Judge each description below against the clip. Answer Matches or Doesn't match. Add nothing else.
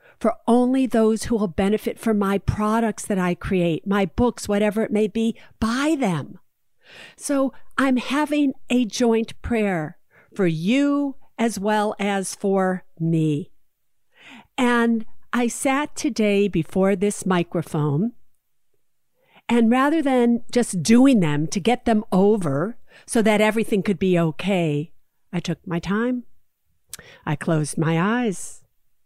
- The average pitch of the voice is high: Matches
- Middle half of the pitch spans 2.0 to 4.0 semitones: Doesn't match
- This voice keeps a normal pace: Doesn't match